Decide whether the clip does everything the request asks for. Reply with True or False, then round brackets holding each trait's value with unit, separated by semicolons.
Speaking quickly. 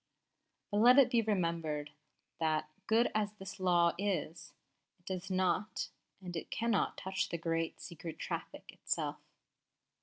False (140 wpm)